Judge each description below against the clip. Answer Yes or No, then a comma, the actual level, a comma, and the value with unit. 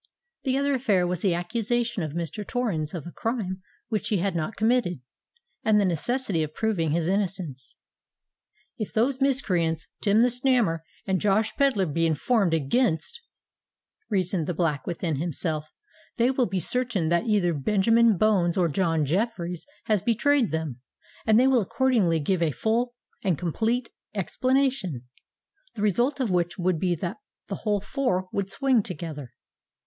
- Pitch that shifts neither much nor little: No, wide, 5.7 semitones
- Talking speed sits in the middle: Yes, average, 155 wpm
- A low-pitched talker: No, high, 195 Hz